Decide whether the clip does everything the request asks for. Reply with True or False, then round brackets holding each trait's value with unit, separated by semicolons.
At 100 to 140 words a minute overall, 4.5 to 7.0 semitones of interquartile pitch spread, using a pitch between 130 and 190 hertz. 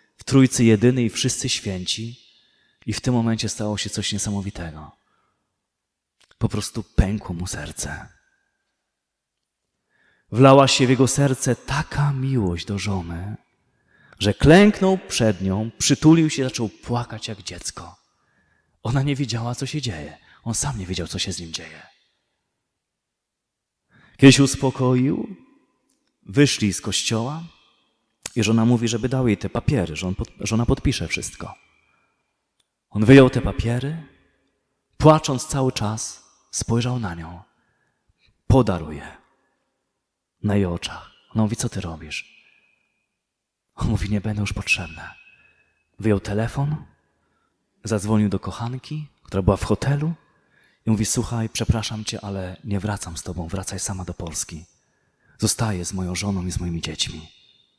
False (135 wpm; 5.1 semitones; 110 Hz)